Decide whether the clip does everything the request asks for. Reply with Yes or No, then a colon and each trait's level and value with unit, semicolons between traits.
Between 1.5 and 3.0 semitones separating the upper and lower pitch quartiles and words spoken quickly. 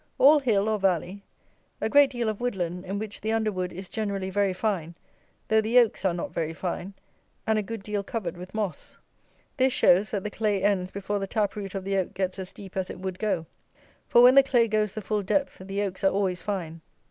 Yes: narrow, 2.6 semitones; fast, 230 wpm